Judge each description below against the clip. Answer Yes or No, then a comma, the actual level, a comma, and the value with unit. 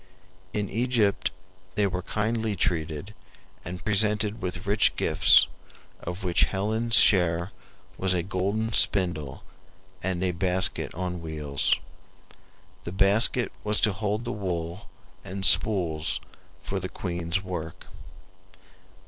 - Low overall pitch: Yes, very low, 95 Hz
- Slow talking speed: Yes, slow, 115 wpm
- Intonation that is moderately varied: Yes, average, 3.3 semitones